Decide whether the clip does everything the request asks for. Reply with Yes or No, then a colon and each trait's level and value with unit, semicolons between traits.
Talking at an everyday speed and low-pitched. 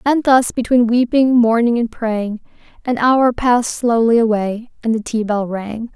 No: average, 170 wpm; high, 230 Hz